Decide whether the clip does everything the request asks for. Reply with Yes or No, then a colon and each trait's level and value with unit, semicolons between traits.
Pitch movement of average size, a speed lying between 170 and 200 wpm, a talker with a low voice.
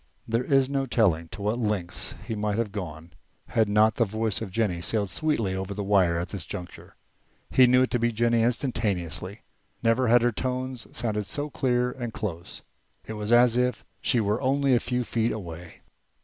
Yes: average, 3.8 semitones; average, 190 wpm; low, 110 Hz